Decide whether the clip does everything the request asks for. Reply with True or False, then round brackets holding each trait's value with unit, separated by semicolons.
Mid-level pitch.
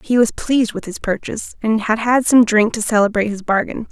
False (220 Hz)